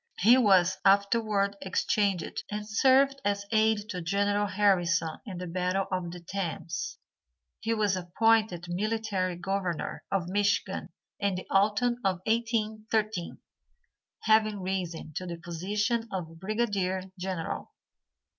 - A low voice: No, high, 200 Hz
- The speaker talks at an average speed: No, slow, 120 wpm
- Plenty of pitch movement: No, average, 3.0 semitones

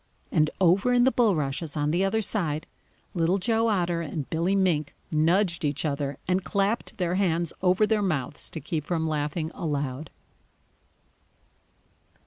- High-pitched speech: No, medium, 170 Hz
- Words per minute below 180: Yes, average, 145 wpm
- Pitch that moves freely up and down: No, average, 4.2 semitones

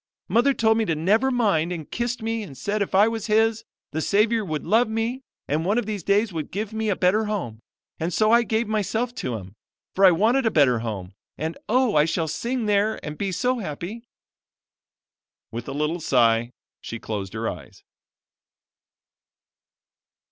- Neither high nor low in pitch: No, high, 200 Hz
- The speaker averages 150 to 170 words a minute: No, average, 185 wpm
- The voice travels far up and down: Yes, wide, 6.6 semitones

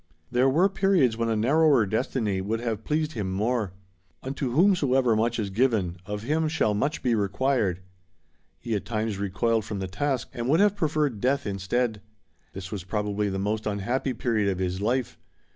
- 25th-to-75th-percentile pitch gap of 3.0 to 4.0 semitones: No, average, 4.6 semitones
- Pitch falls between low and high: No, low, 115 Hz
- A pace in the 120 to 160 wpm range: No, average, 175 wpm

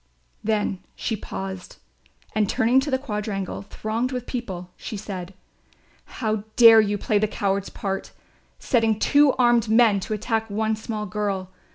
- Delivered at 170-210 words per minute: No, average, 150 wpm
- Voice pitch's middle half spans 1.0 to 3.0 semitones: Yes, narrow, 2.5 semitones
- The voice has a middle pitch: No, high, 215 Hz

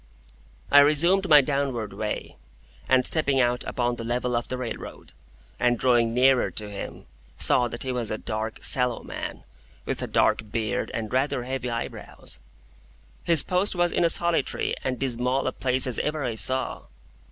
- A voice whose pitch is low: Yes, low, 125 Hz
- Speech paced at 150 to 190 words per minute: Yes, average, 170 wpm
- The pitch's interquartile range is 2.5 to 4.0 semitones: Yes, average, 2.8 semitones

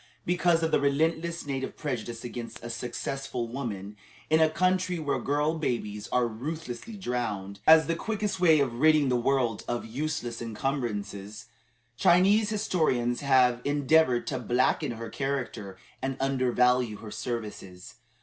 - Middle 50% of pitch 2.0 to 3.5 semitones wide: No, average, 5.1 semitones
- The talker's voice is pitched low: Yes, low, 130 Hz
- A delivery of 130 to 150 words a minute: Yes, average, 140 wpm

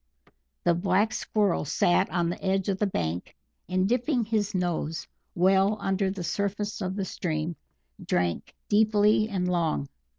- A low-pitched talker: No, high, 190 Hz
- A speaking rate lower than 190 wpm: Yes, average, 145 wpm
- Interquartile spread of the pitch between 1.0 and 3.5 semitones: Yes, average, 3.0 semitones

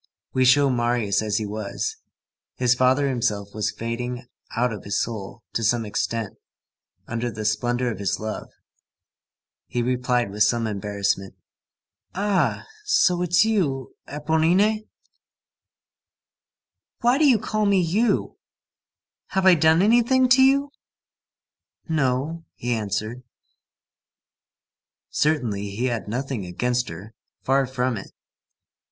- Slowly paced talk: Yes, slow, 120 wpm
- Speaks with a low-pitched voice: Yes, low, 125 Hz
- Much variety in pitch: Yes, wide, 7.0 semitones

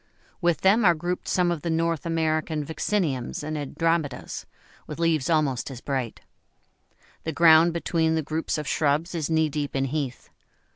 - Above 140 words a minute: Yes, average, 160 wpm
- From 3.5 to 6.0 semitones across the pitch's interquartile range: No, narrow, 2.5 semitones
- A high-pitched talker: No, medium, 160 Hz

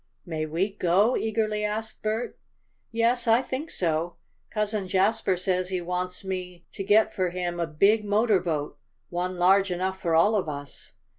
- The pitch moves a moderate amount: Yes, average, 3.4 semitones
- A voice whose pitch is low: No, high, 190 Hz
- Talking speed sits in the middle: Yes, average, 165 wpm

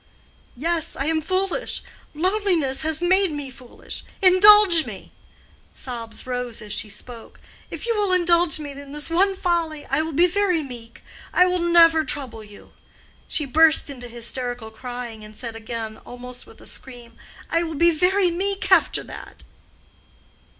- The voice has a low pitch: No, very high, 310 Hz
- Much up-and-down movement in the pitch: Yes, wide, 6.4 semitones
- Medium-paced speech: Yes, average, 145 wpm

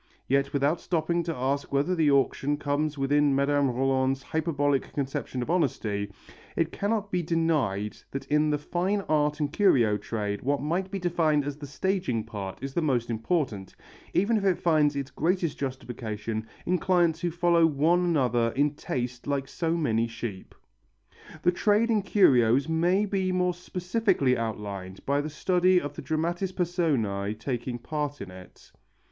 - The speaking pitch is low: No, medium, 145 Hz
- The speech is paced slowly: No, average, 165 wpm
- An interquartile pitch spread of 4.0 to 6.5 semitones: Yes, wide, 5.5 semitones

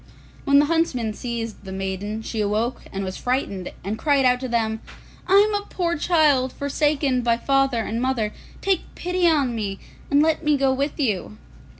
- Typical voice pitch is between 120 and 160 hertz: No, very high, 255 Hz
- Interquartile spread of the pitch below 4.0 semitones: No, average, 5.1 semitones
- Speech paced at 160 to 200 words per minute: Yes, average, 185 wpm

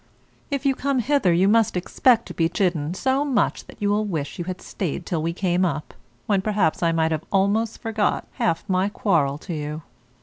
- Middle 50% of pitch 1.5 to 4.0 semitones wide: No, average, 4.7 semitones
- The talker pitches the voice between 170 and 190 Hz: Yes, medium, 185 Hz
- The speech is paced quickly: Yes, fast, 210 wpm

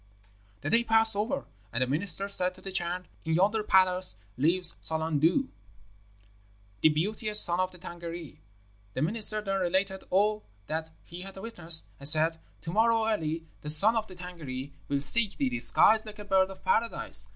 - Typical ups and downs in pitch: Yes, average, 4.7 semitones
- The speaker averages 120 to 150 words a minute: No, average, 175 wpm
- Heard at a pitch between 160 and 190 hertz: Yes, medium, 185 Hz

